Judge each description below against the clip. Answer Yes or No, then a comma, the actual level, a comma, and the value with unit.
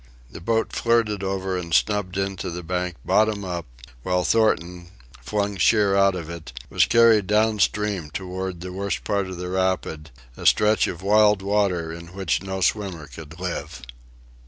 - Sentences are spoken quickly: No, average, 170 wpm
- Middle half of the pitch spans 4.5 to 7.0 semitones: No, average, 2.8 semitones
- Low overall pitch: Yes, very low, 95 Hz